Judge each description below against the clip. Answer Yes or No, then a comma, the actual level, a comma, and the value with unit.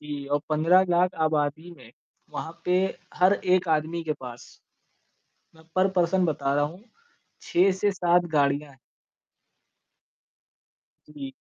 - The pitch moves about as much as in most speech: Yes, average, 3.7 semitones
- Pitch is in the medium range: Yes, medium, 165 Hz